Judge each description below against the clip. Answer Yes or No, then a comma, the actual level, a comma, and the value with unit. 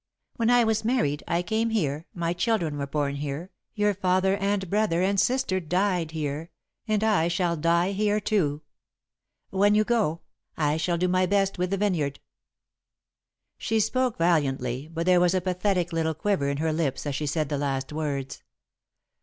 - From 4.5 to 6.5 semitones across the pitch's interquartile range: Yes, average, 4.9 semitones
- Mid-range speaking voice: Yes, medium, 175 Hz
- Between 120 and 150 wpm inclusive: No, average, 175 wpm